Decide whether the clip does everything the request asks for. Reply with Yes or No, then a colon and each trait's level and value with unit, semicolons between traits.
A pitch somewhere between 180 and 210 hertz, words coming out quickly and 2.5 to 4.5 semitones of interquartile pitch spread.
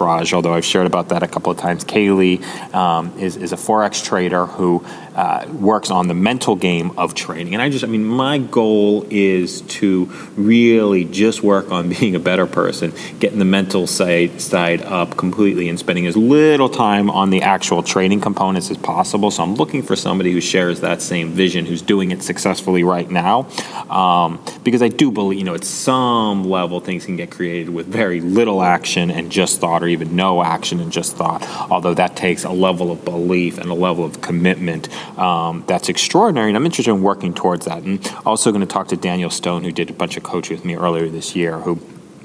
No: very low, 90 Hz; fast, 210 wpm; average, 2.8 semitones